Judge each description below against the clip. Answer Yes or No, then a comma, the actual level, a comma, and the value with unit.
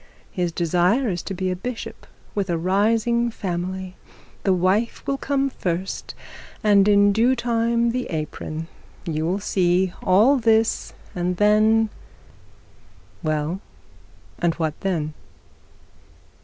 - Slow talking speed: Yes, slow, 125 wpm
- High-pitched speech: Yes, high, 195 Hz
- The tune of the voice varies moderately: Yes, average, 4.3 semitones